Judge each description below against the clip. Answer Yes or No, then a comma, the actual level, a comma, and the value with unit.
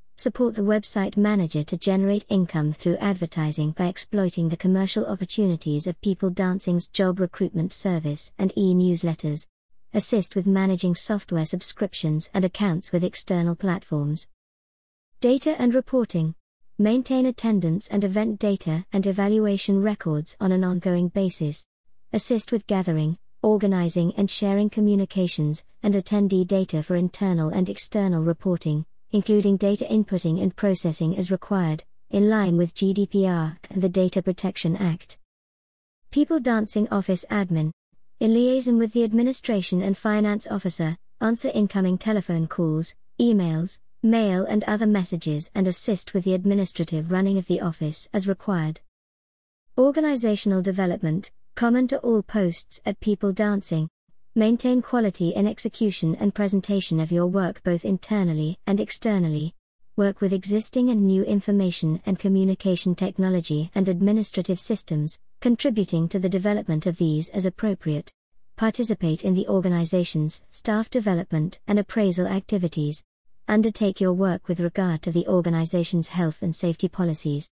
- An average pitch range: Yes, average, 3.3 semitones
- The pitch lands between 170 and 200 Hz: Yes, high, 190 Hz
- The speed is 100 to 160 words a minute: Yes, slow, 135 wpm